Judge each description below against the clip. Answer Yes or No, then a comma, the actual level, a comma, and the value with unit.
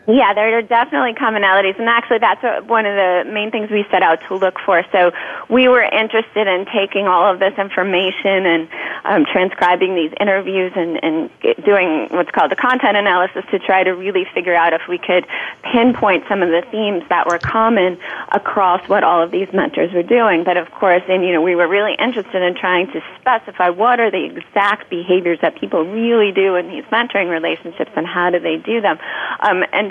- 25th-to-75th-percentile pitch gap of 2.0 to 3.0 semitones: No, average, 3.5 semitones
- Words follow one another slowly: No, fast, 205 wpm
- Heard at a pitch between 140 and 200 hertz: Yes, high, 190 Hz